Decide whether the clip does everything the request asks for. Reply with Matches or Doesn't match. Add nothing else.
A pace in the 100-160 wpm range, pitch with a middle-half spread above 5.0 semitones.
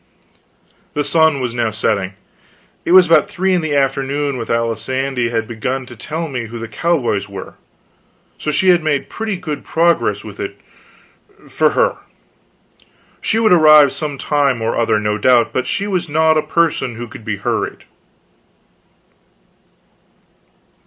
Matches